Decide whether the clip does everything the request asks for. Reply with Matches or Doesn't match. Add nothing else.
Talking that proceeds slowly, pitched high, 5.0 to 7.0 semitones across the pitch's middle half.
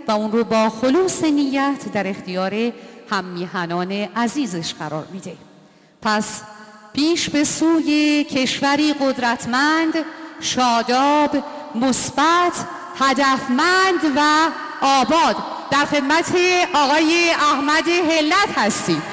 Matches